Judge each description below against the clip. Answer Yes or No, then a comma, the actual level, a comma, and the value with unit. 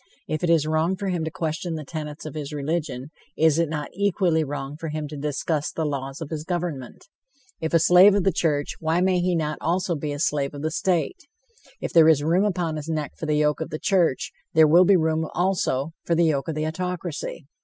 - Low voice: No, medium, 160 Hz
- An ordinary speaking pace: No, fast, 230 wpm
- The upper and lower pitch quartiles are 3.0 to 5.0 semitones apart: No, narrow, 2.6 semitones